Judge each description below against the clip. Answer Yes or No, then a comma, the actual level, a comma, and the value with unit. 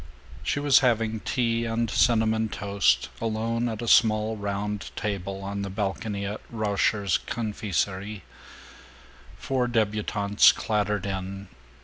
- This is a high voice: No, low, 105 Hz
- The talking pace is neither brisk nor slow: No, slow, 115 wpm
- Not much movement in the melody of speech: Yes, narrow, 2.1 semitones